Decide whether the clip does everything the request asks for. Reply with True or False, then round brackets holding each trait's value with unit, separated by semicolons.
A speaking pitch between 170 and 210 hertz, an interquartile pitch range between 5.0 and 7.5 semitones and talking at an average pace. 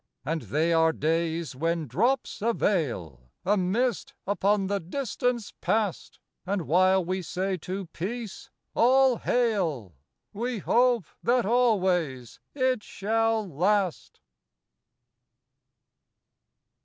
False (190 Hz; 5.6 semitones; 120 wpm)